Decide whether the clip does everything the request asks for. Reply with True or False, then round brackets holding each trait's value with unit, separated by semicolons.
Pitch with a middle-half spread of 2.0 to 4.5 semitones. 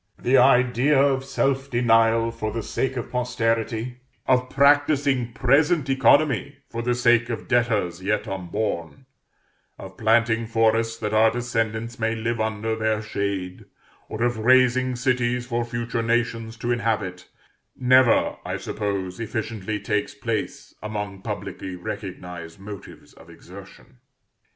True (2.6 semitones)